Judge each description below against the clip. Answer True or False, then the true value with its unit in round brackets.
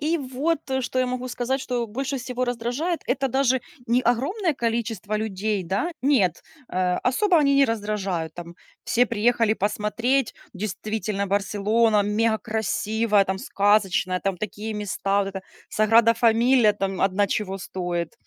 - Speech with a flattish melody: False (3.9 semitones)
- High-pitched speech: True (220 Hz)